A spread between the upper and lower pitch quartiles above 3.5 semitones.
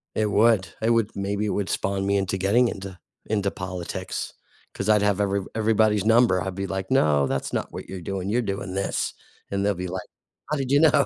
No: narrow, 2.4 semitones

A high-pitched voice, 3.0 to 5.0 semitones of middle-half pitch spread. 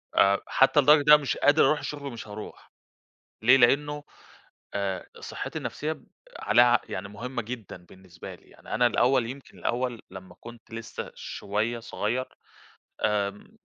No: low, 120 Hz; average, 4.6 semitones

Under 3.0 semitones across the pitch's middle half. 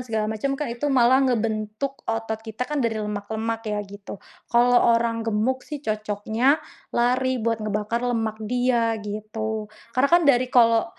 Yes: narrow, 2.6 semitones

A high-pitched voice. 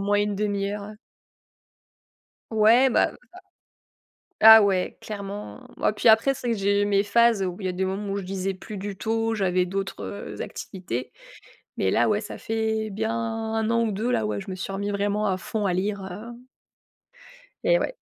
Yes: high, 205 Hz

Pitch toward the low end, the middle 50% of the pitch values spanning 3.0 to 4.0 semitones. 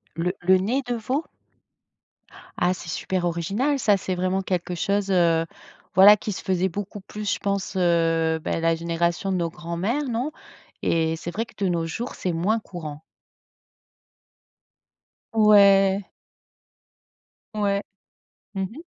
No: high, 190 Hz; average, 3.3 semitones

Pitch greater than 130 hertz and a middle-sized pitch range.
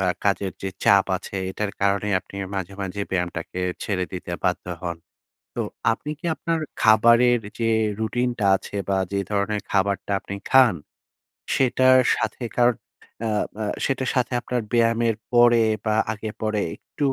No: low, 110 Hz; average, 3.4 semitones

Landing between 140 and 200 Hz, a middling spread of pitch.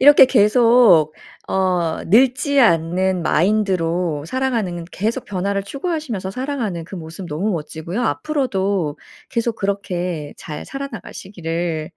No: high, 190 Hz; wide, 6.0 semitones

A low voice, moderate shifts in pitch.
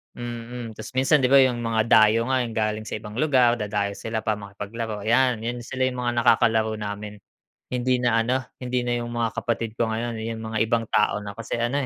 No: low, 115 Hz; narrow, 2.0 semitones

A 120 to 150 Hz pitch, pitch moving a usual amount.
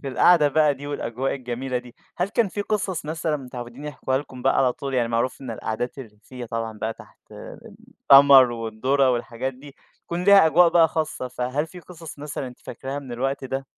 Yes: low, 135 Hz; average, 3.5 semitones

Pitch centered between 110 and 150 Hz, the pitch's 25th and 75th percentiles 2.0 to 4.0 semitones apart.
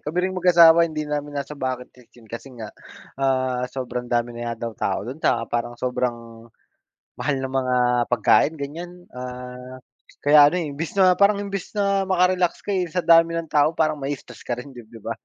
No: medium, 140 Hz; average, 5.0 semitones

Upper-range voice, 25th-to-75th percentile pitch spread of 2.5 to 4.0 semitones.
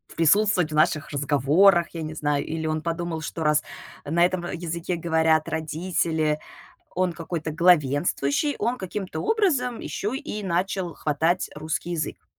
No: medium, 165 Hz; average, 2.8 semitones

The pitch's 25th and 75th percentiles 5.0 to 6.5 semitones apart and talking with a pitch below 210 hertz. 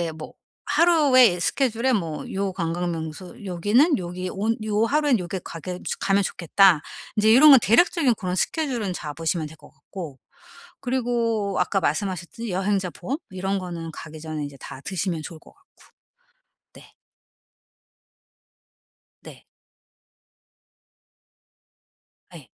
Yes: wide, 5.4 semitones; high, 190 Hz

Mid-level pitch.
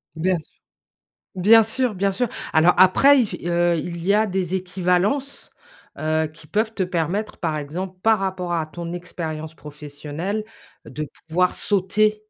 Yes: medium, 180 Hz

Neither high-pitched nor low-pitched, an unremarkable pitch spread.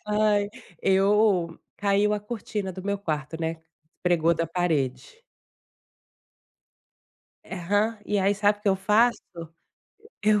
No: high, 200 Hz; average, 3.6 semitones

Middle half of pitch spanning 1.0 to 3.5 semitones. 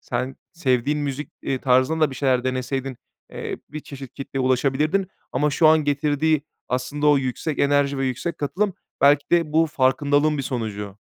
Yes: narrow, 2.6 semitones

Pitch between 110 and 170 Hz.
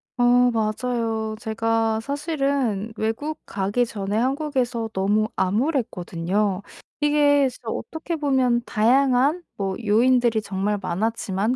No: high, 225 Hz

